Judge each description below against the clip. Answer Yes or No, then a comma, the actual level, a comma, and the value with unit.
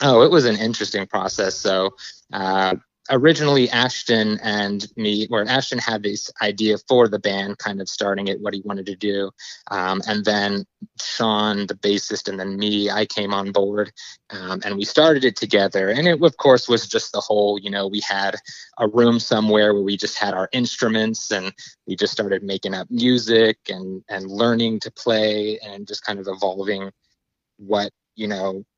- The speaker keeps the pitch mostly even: Yes, narrow, 2.0 semitones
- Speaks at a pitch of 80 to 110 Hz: Yes, low, 105 Hz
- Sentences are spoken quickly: No, average, 185 wpm